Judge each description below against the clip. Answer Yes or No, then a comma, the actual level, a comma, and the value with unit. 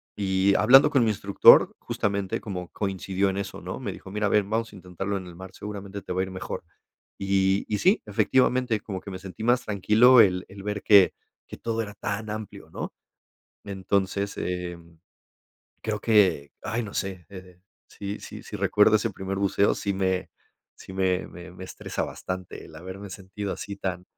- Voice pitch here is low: Yes, low, 100 Hz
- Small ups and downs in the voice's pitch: Yes, narrow, 2.0 semitones